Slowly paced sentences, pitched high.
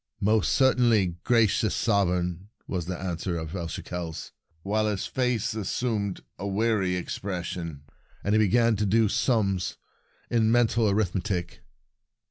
No: slow, 130 wpm; low, 100 Hz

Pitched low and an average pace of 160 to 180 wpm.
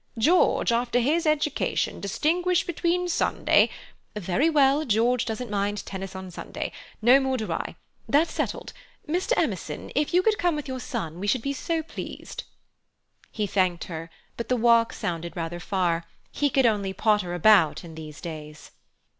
No: high, 230 Hz; average, 165 wpm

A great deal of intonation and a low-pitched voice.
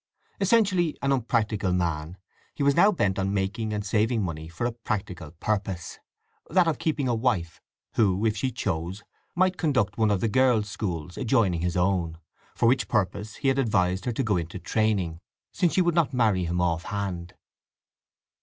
Yes: wide, 5.8 semitones; low, 105 Hz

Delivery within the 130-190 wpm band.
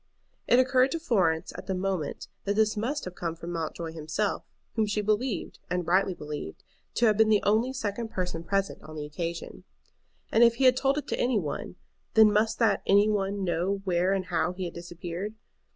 No: average, 200 wpm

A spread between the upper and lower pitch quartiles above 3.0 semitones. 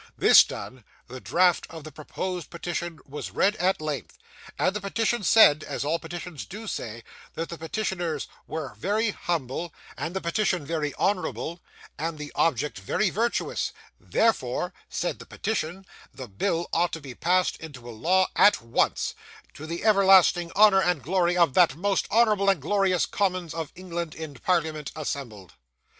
Yes: average, 4.1 semitones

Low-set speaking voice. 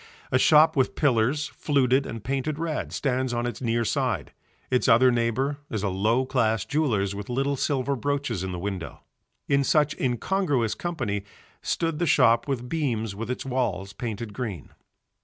Yes: low, 125 Hz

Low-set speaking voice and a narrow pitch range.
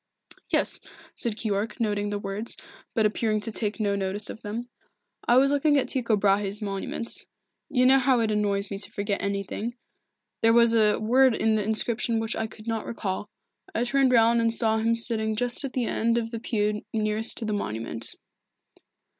No: high, 220 Hz; narrow, 2.2 semitones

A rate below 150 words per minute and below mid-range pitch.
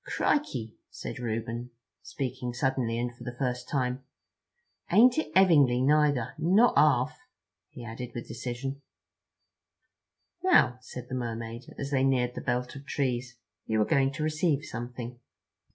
Yes: average, 140 wpm; low, 125 Hz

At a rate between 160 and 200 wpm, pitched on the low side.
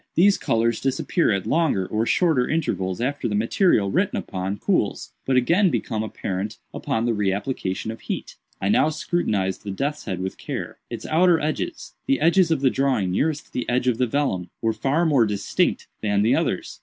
Yes: average, 180 wpm; low, 120 Hz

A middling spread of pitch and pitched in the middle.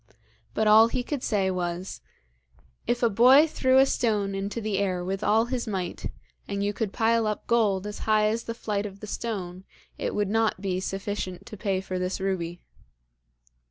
No: average, 3.0 semitones; high, 205 Hz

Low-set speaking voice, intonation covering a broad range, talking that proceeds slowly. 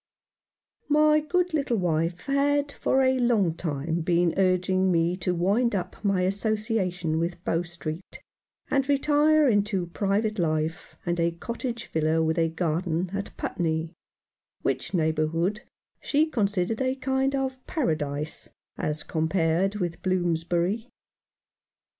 No: medium, 185 Hz; wide, 6.3 semitones; slow, 130 wpm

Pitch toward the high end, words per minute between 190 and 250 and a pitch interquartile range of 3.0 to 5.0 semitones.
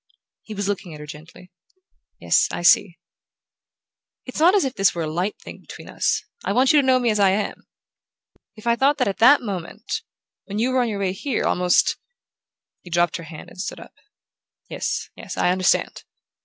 No: high, 200 Hz; fast, 205 wpm; wide, 5.6 semitones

